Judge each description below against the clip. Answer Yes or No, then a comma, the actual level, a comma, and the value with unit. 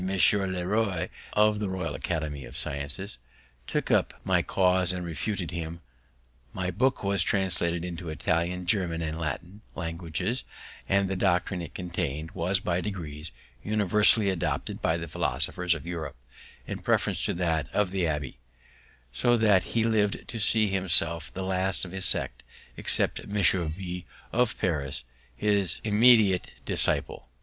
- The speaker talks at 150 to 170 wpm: Yes, average, 155 wpm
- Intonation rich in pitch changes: No, average, 3.1 semitones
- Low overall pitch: Yes, very low, 90 Hz